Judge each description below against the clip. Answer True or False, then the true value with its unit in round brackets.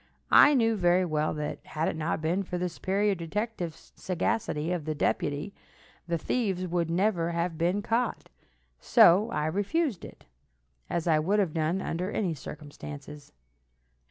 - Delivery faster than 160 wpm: False (155 wpm)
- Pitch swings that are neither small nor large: True (4.1 semitones)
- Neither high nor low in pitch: True (175 Hz)